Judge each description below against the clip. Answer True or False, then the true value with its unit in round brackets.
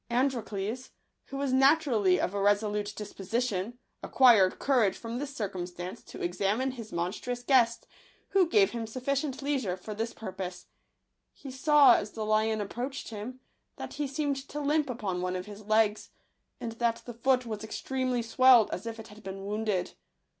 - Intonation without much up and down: False (4.2 semitones)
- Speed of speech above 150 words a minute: True (170 wpm)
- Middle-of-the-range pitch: False (230 Hz)